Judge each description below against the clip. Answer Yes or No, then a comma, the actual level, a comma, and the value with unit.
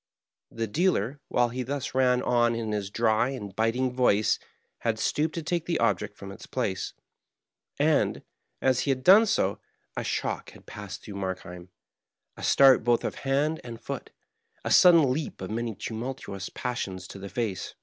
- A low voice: Yes, low, 120 Hz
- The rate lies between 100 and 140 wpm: No, average, 180 wpm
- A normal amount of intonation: Yes, average, 4.5 semitones